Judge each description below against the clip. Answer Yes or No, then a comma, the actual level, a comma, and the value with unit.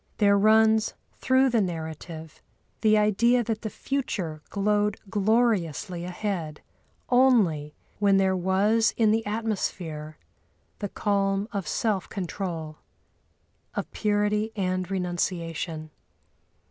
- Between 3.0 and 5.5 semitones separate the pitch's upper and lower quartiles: Yes, average, 3.8 semitones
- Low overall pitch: No, high, 200 Hz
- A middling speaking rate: No, slow, 105 wpm